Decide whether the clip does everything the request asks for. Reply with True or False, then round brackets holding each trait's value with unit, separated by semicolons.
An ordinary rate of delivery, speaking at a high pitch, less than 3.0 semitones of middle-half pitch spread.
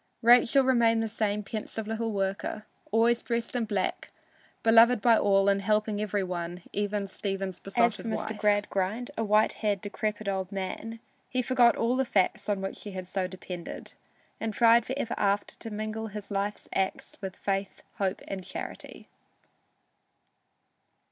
True (165 wpm; 210 Hz; 2.5 semitones)